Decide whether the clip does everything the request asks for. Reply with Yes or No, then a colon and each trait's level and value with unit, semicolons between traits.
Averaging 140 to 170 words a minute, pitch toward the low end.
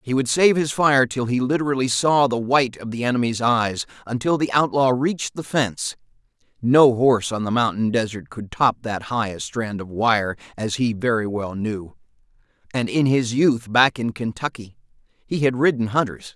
No: average, 185 wpm; low, 120 Hz